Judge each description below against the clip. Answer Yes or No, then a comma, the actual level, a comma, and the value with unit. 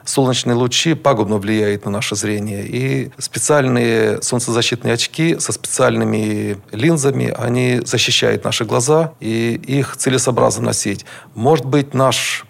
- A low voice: Yes, low, 125 Hz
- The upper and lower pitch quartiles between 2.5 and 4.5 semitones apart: Yes, average, 3.5 semitones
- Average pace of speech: Yes, average, 120 wpm